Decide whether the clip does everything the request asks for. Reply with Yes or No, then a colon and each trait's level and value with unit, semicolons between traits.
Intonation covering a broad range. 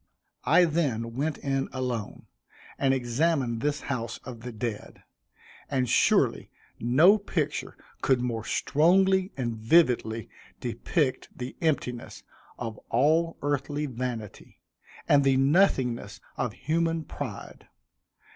No: average, 4.6 semitones